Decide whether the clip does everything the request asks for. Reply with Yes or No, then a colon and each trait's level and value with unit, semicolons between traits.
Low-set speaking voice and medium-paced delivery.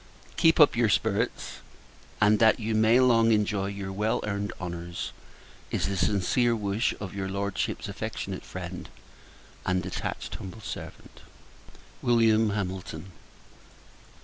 No: low, 105 Hz; slow, 120 wpm